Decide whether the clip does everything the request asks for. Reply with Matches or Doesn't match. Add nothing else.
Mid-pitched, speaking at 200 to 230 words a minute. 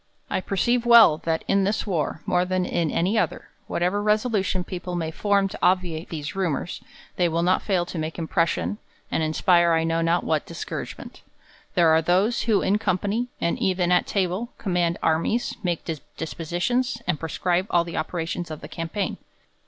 Doesn't match